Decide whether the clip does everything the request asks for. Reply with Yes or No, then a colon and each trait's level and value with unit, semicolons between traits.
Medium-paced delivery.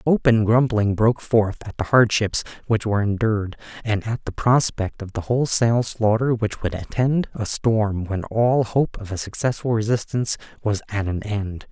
Yes: average, 175 wpm